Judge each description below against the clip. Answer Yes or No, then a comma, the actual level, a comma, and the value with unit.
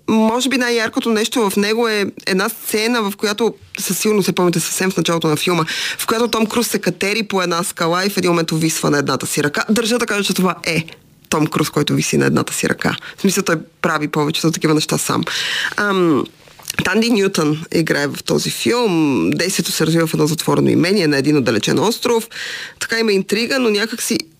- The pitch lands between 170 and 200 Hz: Yes, medium, 185 Hz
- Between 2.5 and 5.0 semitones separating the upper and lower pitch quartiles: No, wide, 5.4 semitones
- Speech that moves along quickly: Yes, fast, 210 wpm